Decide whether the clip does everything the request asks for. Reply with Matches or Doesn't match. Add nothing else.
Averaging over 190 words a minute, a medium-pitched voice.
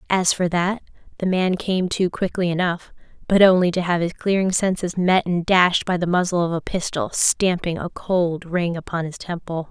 Matches